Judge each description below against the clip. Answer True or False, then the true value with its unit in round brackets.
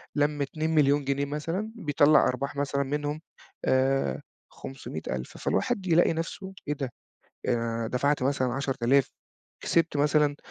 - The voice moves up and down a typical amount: False (2.2 semitones)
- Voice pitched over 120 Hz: True (140 Hz)